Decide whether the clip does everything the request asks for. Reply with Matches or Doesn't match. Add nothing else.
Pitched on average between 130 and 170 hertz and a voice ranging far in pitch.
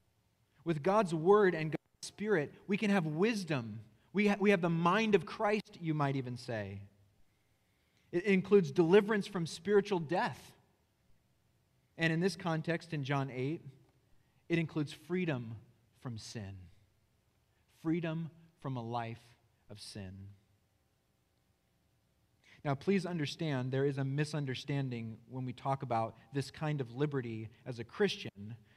Matches